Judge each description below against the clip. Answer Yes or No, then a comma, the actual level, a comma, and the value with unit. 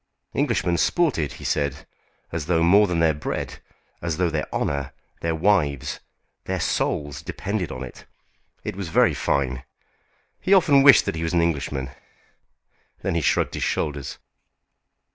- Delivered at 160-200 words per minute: No, average, 150 wpm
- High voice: No, very low, 80 Hz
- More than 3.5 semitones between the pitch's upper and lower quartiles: Yes, average, 4.1 semitones